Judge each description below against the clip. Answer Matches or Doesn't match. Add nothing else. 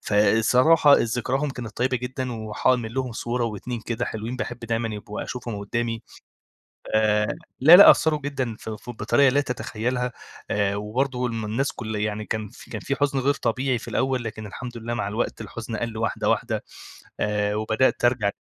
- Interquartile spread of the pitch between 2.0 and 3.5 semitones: Matches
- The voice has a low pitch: Matches